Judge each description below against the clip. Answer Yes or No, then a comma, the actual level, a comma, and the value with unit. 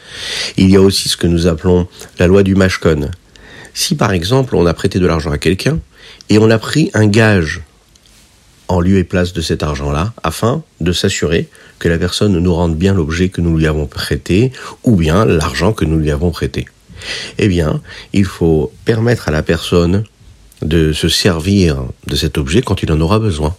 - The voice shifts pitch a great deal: No, average, 3.7 semitones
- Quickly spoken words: No, average, 195 wpm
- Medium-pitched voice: No, very low, 90 Hz